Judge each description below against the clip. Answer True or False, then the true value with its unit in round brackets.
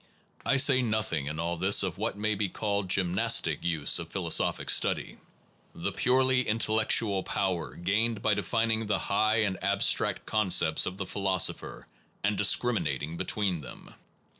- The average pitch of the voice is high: False (100 Hz)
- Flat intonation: False (3.4 semitones)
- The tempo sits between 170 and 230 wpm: False (160 wpm)